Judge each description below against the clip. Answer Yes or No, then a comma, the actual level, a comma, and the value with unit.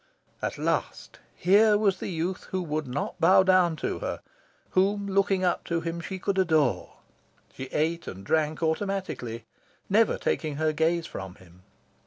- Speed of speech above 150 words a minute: Yes, average, 160 wpm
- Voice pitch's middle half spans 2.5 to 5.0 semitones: Yes, average, 3.9 semitones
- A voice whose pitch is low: No, medium, 170 Hz